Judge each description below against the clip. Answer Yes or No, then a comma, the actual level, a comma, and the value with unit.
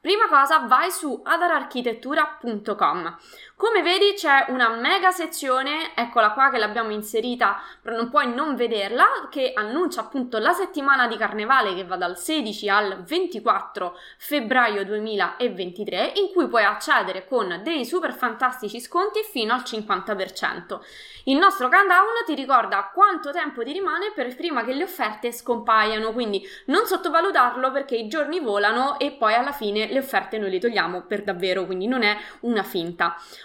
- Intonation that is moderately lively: No, wide, 6.7 semitones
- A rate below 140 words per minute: No, average, 155 wpm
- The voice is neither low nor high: No, very high, 250 Hz